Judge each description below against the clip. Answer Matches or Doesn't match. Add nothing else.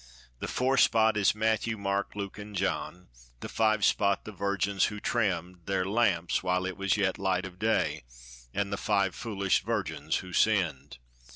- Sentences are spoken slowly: Doesn't match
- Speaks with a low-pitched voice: Matches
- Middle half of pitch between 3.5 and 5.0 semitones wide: Doesn't match